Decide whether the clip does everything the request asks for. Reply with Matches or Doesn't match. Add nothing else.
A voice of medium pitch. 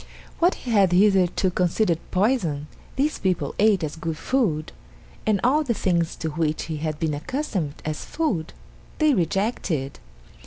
Matches